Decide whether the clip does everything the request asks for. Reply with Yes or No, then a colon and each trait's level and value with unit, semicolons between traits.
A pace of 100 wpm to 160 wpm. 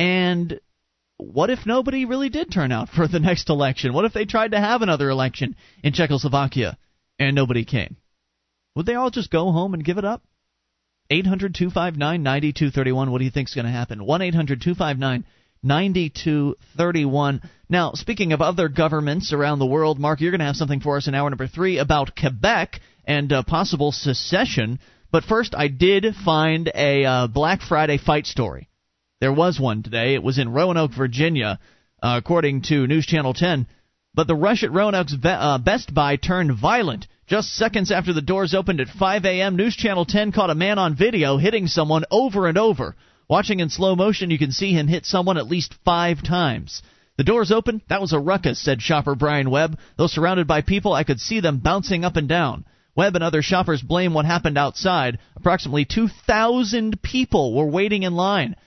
No: average, 190 wpm